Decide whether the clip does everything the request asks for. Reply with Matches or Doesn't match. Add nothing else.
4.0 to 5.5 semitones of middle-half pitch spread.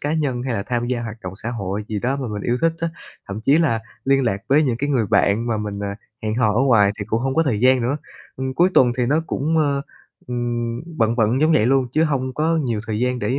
Doesn't match